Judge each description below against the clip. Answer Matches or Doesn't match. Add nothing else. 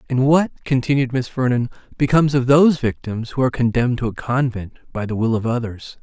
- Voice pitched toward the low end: Matches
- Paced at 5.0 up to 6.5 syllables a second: Matches